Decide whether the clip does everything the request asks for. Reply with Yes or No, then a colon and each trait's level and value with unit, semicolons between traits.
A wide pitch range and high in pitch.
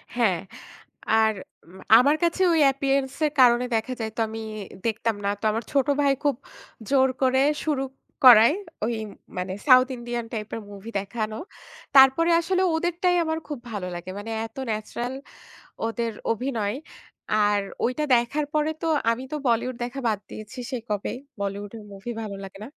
No: average, 4.1 semitones; high, 240 Hz